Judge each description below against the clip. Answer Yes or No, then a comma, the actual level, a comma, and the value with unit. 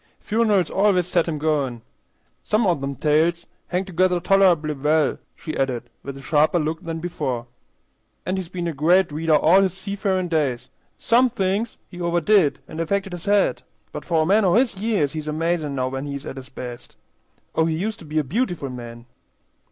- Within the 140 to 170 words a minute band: No, average, 190 wpm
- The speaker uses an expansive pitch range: No, average, 4.3 semitones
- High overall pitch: No, medium, 165 Hz